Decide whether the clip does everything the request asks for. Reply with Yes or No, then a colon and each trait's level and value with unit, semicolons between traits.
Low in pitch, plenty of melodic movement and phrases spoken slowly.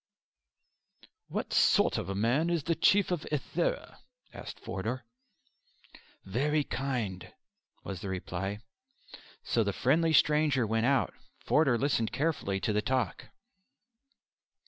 Yes: low, 130 Hz; wide, 6.5 semitones; slow, 120 wpm